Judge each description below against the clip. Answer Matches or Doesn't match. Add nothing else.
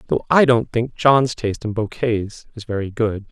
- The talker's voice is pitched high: Doesn't match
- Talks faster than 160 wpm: Matches